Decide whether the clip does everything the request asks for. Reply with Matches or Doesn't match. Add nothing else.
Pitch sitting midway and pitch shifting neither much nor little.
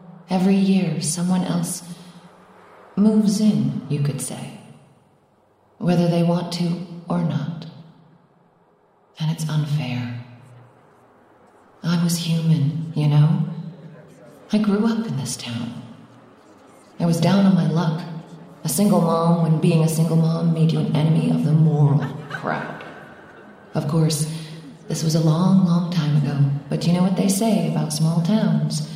Doesn't match